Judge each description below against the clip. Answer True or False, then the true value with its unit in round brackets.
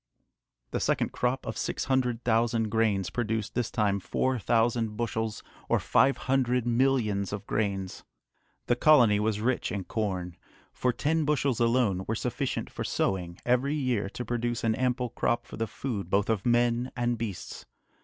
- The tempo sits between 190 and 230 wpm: False (165 wpm)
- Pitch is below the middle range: True (115 Hz)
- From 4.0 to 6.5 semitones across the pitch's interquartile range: False (2.9 semitones)